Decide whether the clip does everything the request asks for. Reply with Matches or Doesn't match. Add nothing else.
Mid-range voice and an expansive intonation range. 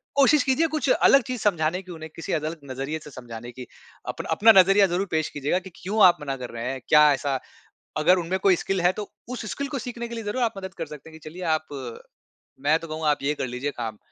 Matches